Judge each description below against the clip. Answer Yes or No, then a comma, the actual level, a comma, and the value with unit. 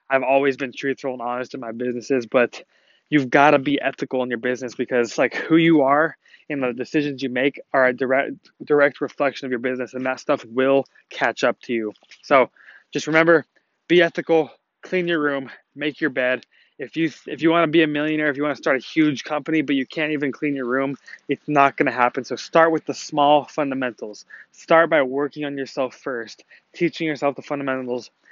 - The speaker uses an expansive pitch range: No, narrow, 2.6 semitones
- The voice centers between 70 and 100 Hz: No, medium, 140 Hz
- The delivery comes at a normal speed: No, fast, 210 wpm